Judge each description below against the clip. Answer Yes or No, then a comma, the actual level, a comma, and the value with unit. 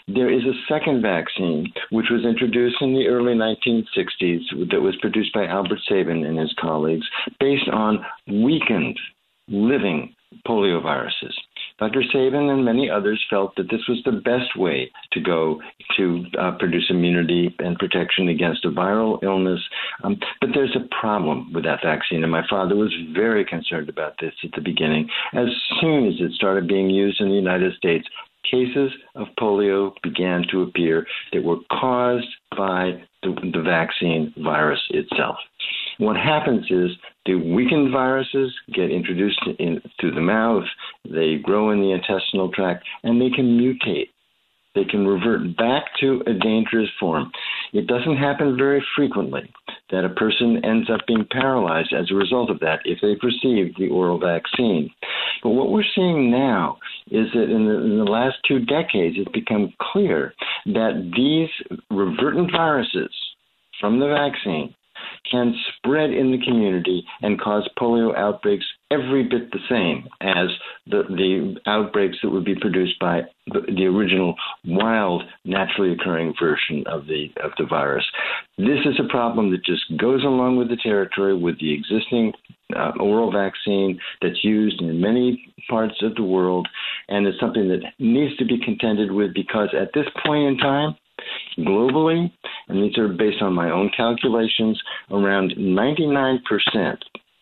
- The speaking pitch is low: Yes, low, 110 Hz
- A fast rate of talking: No, average, 160 wpm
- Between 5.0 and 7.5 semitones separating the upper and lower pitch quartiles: Yes, average, 5.3 semitones